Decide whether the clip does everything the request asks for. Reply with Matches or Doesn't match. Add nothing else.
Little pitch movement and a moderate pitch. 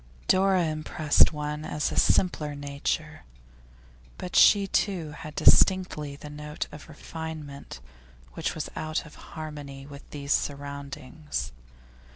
Matches